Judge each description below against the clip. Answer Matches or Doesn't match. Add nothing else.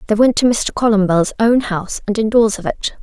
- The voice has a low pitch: Doesn't match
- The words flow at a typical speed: Doesn't match